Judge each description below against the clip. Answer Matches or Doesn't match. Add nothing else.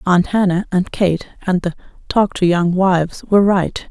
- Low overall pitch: Doesn't match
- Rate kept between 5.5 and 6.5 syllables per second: Doesn't match